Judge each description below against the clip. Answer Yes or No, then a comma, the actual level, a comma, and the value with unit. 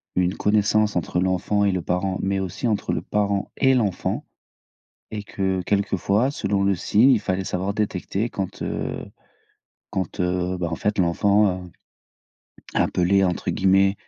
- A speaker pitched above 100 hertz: No, very low, 95 Hz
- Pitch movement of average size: No, narrow, 2.1 semitones